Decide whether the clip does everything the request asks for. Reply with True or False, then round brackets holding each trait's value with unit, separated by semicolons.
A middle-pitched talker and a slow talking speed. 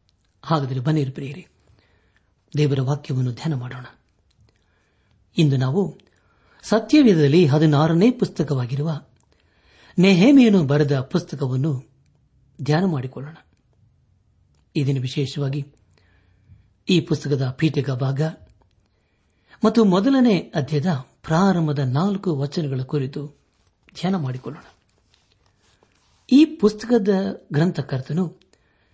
False (145 Hz; 75 wpm)